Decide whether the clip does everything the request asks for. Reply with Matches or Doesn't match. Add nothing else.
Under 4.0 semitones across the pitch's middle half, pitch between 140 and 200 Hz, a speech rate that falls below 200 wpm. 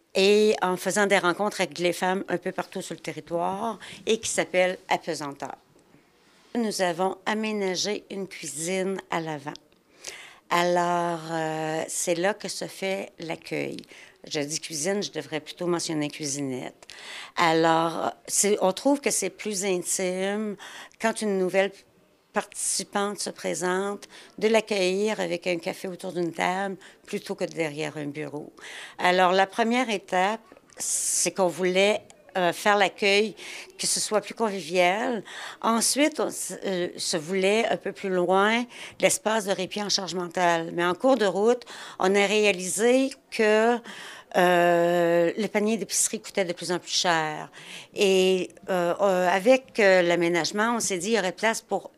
Matches